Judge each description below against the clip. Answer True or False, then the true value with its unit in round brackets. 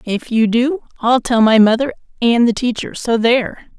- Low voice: False (235 Hz)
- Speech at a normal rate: True (190 wpm)